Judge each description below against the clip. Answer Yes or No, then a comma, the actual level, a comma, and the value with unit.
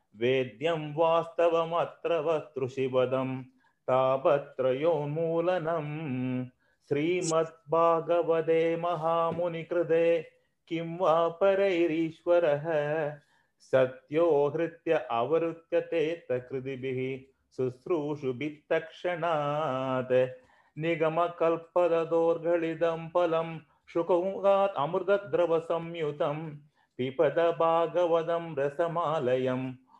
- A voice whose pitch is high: No, medium, 165 Hz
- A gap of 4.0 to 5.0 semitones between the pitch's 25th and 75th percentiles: No, average, 3.3 semitones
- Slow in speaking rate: Yes, slow, 45 wpm